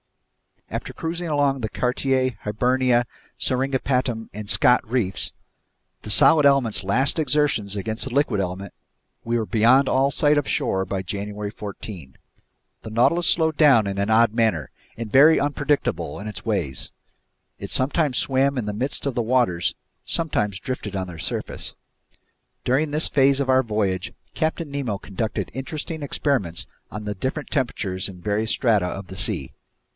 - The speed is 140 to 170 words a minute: Yes, average, 155 wpm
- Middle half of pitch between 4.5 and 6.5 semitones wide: Yes, average, 5.2 semitones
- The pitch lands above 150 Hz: No, low, 120 Hz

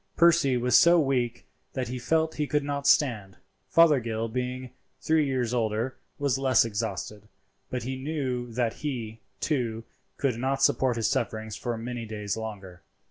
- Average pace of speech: Yes, average, 155 wpm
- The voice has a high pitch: No, low, 125 Hz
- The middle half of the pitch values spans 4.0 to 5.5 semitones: No, average, 3.5 semitones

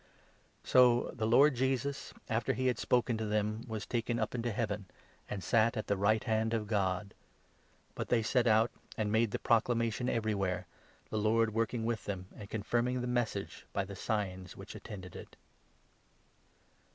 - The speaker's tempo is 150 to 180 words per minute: Yes, average, 175 wpm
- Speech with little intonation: Yes, narrow, 2.3 semitones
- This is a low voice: Yes, low, 110 Hz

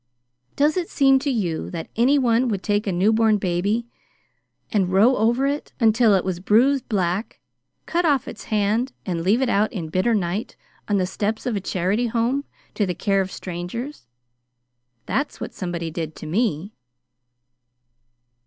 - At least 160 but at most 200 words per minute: Yes, average, 165 wpm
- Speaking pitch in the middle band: No, high, 210 Hz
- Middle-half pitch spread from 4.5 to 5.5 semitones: Yes, average, 4.8 semitones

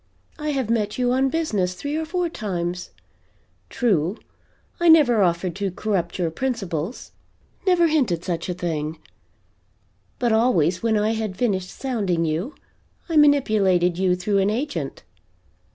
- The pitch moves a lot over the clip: Yes, wide, 6.4 semitones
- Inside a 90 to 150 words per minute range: Yes, average, 140 wpm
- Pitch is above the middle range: Yes, high, 210 Hz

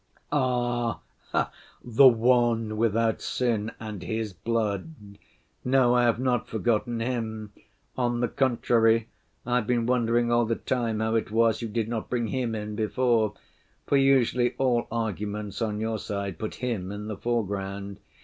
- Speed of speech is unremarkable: Yes, average, 150 wpm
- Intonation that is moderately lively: No, narrow, 2.1 semitones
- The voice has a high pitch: No, low, 115 Hz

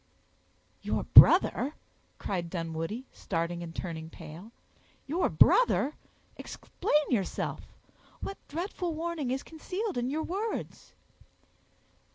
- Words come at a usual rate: No, slow, 95 wpm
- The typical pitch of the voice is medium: No, very high, 260 Hz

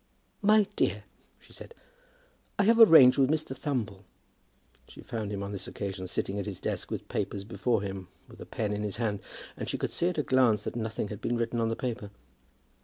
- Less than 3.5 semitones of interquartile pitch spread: No, average, 4.4 semitones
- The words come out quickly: Yes, fast, 210 wpm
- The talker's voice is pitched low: Yes, low, 110 Hz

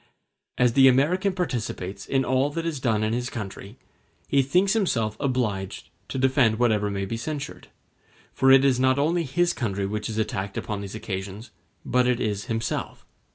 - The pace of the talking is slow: No, average, 175 wpm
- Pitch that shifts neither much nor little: Yes, average, 4.5 semitones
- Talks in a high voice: No, low, 125 Hz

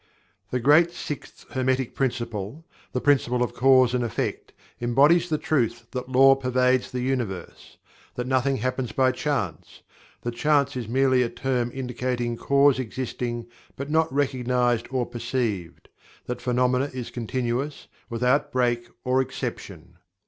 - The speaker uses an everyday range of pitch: No, narrow, 1.9 semitones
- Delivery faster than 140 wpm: No, slow, 135 wpm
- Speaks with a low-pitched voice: Yes, low, 125 Hz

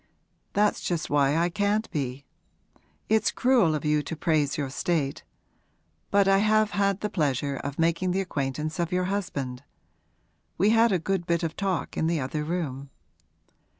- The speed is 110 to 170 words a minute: Yes, average, 165 wpm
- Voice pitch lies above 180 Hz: No, medium, 170 Hz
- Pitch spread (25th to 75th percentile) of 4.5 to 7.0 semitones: Yes, average, 5.2 semitones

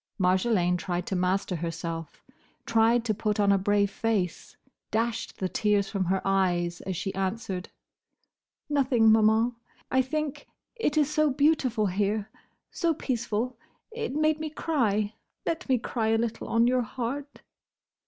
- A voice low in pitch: No, high, 220 Hz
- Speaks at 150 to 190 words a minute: No, slow, 135 wpm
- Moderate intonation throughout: Yes, average, 5.0 semitones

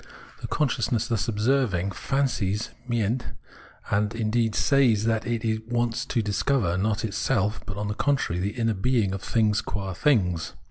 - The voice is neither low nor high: No, low, 110 Hz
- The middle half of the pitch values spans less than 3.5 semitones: Yes, average, 2.8 semitones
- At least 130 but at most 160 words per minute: Yes, average, 150 wpm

